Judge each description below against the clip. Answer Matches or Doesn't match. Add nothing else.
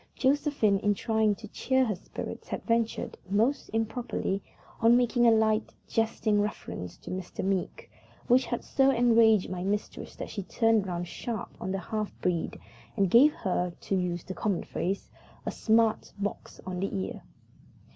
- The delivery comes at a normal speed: Matches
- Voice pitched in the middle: Doesn't match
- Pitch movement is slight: Doesn't match